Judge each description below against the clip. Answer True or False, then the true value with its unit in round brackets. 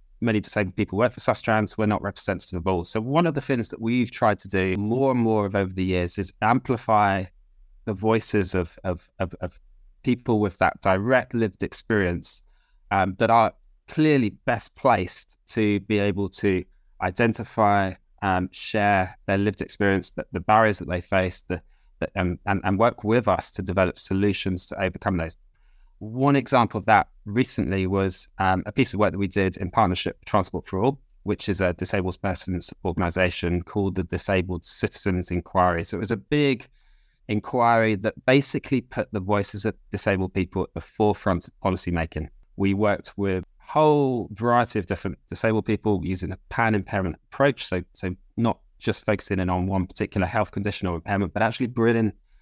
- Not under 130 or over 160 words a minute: False (185 wpm)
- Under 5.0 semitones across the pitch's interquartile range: True (3.2 semitones)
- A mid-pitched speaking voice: False (100 Hz)